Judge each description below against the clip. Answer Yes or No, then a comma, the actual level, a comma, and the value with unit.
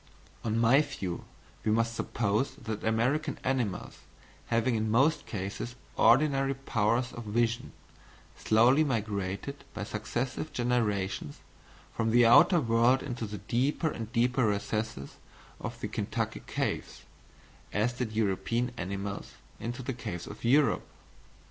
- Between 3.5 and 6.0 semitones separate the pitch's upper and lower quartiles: No, average, 3.0 semitones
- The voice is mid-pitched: No, low, 115 Hz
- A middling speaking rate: No, slow, 125 wpm